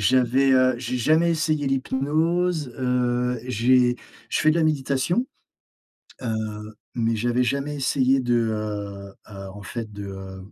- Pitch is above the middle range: No, low, 125 Hz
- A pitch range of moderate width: Yes, average, 4.0 semitones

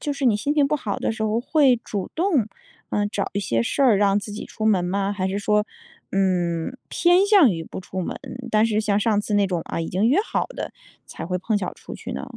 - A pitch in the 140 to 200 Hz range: No, high, 210 Hz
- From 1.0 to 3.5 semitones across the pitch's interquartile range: No, average, 4.1 semitones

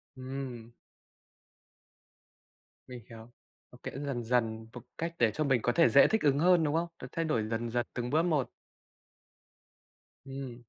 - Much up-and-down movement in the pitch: No, average, 4.1 semitones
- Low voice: Yes, low, 130 Hz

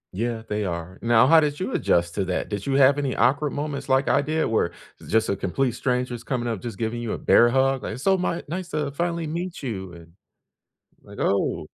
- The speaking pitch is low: Yes, low, 125 Hz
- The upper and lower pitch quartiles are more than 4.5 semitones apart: Yes, average, 5.1 semitones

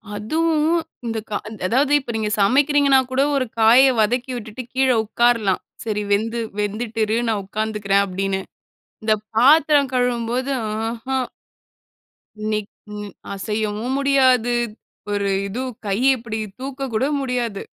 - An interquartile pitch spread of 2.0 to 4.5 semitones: Yes, average, 3.7 semitones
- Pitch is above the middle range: Yes, high, 230 Hz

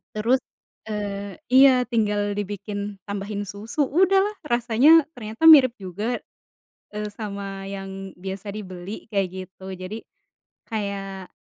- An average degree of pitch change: Yes, average, 3.1 semitones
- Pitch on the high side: Yes, high, 205 Hz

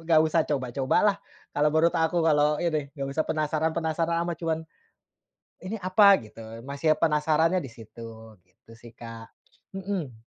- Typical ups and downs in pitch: Yes, average, 4.1 semitones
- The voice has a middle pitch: Yes, medium, 155 Hz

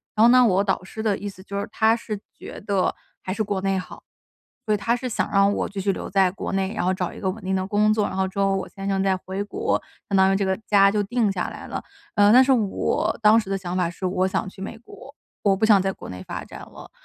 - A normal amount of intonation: No, narrow, 2.0 semitones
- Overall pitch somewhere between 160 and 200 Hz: Yes, high, 195 Hz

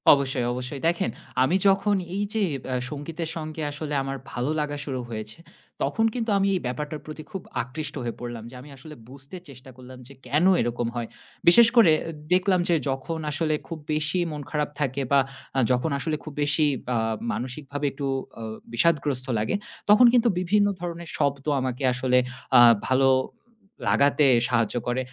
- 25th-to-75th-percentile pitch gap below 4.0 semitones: No, average, 4.4 semitones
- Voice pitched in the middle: Yes, medium, 145 Hz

